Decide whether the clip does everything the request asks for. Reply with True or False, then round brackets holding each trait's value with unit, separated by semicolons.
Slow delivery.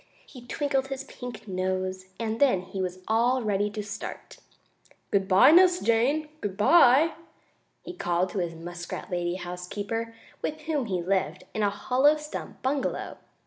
False (155 wpm)